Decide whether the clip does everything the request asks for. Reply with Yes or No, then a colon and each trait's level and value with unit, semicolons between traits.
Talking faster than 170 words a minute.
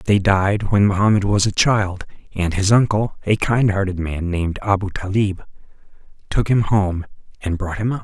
Yes: average, 185 wpm